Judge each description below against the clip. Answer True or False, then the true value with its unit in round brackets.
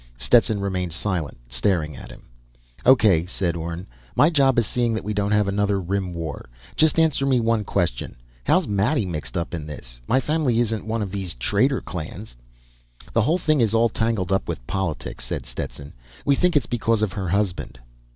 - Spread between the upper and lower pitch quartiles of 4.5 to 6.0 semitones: True (5.1 semitones)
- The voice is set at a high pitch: False (100 Hz)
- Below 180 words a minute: False (190 wpm)